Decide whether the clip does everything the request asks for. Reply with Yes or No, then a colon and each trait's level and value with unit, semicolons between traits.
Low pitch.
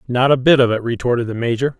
Yes: low, 125 Hz